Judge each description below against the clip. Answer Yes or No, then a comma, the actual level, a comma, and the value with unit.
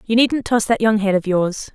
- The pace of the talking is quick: Yes, fast, 275 wpm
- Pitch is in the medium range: No, high, 215 Hz